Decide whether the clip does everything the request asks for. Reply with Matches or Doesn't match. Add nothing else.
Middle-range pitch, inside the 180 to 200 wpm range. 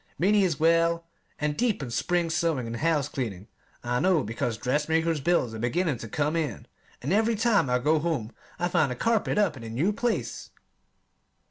Matches